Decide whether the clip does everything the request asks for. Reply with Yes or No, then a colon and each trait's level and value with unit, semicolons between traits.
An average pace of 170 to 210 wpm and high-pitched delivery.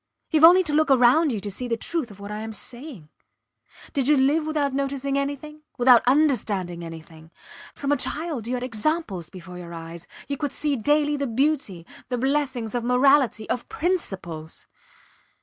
Yes: average, 175 wpm; very high, 255 Hz